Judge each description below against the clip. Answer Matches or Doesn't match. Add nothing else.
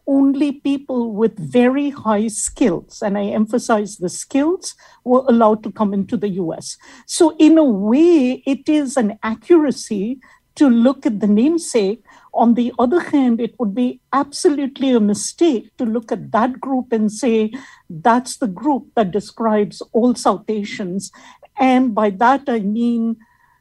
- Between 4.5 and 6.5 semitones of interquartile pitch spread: Doesn't match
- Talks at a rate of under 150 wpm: Doesn't match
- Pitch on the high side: Matches